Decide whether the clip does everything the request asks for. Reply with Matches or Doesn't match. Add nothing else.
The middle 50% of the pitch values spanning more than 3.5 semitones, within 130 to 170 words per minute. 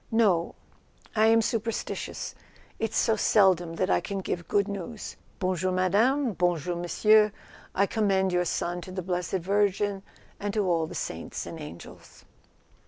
Doesn't match